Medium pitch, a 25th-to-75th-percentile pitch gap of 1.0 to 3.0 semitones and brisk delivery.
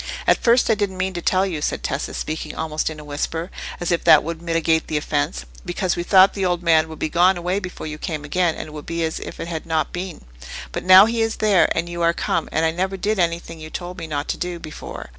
Yes: medium, 170 Hz; average, 2.7 semitones; fast, 265 wpm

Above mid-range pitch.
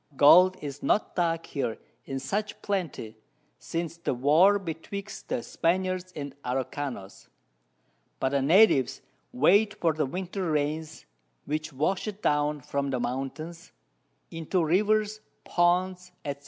No: medium, 165 Hz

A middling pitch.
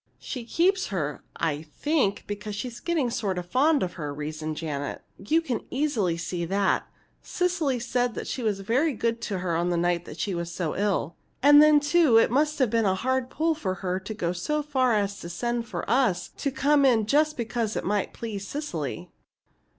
No: high, 225 Hz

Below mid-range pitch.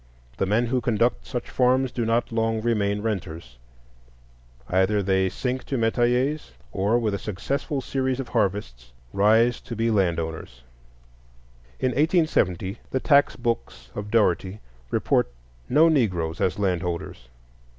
Yes: low, 110 Hz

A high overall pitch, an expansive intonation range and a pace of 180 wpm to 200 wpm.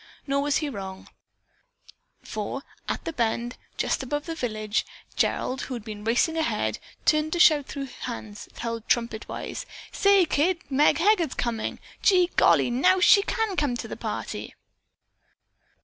No: very high, 275 Hz; wide, 6.1 semitones; average, 150 wpm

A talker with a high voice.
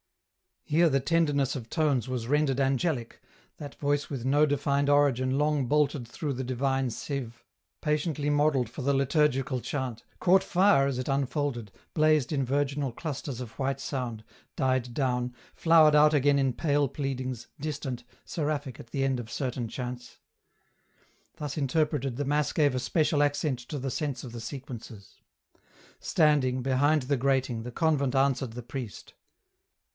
No: low, 135 Hz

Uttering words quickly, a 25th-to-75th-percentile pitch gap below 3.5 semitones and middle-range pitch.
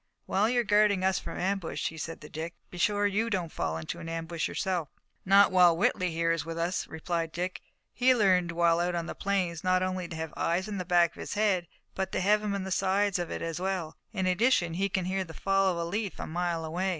Yes: fast, 250 wpm; average, 2.7 semitones; medium, 180 Hz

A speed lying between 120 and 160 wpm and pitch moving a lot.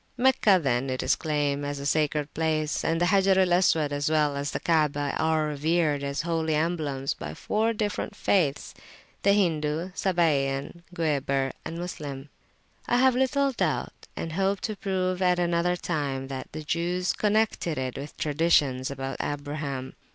No: average, 155 wpm; average, 4.0 semitones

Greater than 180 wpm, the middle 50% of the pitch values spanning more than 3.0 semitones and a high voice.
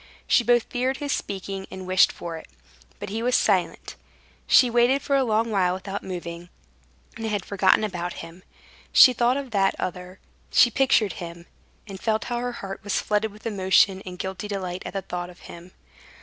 Yes: average, 190 wpm; average, 4.1 semitones; high, 195 Hz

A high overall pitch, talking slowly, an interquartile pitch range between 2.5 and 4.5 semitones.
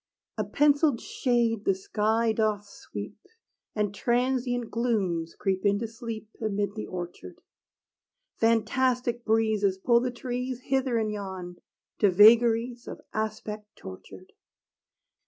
Yes: high, 220 Hz; slow, 120 wpm; average, 2.9 semitones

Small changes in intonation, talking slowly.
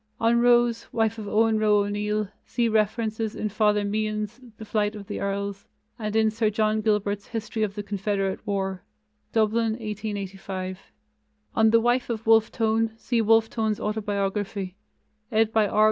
No: narrow, 1.5 semitones; average, 160 wpm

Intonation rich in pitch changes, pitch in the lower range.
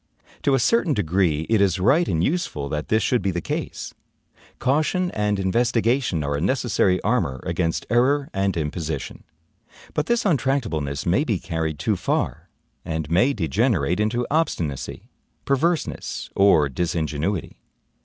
Yes: wide, 8.4 semitones; low, 100 Hz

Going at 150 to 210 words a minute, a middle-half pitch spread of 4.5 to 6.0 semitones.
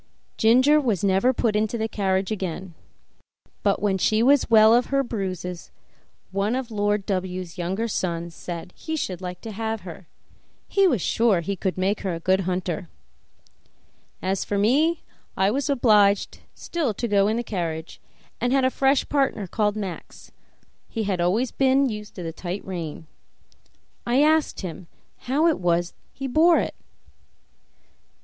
Yes: average, 165 wpm; average, 4.9 semitones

